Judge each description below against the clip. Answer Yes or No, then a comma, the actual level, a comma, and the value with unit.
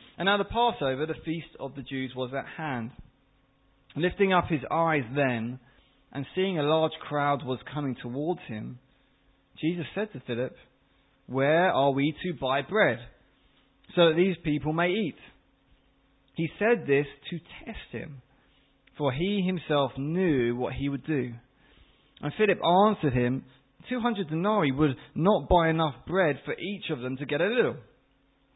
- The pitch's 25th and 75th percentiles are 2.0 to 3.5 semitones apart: No, average, 4.5 semitones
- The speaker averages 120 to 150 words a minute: No, average, 160 wpm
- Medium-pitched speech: Yes, medium, 145 Hz